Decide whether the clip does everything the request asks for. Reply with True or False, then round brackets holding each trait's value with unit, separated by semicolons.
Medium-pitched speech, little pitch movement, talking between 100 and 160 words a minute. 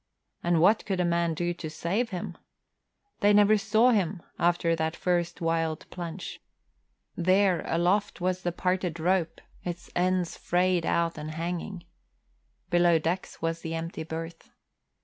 True (175 Hz; 2.0 semitones; 145 wpm)